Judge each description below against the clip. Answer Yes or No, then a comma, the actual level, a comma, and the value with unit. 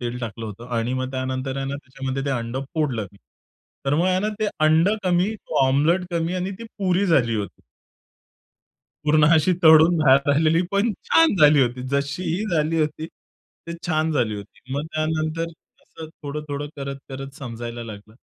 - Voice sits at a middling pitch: Yes, medium, 145 Hz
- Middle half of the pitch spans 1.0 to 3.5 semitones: No, average, 4.0 semitones